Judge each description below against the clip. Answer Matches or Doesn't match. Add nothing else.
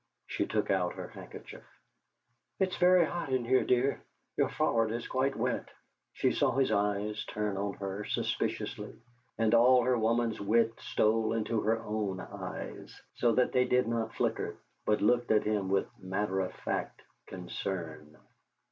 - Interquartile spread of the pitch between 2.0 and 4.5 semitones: Matches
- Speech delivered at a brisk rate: Doesn't match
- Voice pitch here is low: Matches